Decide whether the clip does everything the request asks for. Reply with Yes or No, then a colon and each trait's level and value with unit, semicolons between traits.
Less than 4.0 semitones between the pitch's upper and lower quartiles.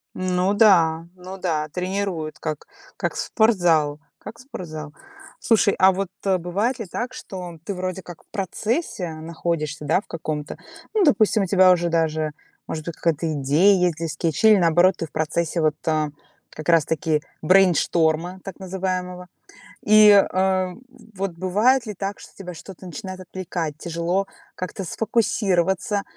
Yes: average, 3.2 semitones